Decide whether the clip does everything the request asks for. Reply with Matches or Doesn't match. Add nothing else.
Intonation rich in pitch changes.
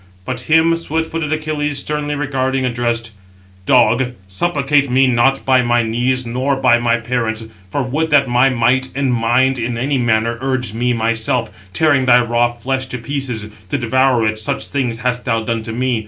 Doesn't match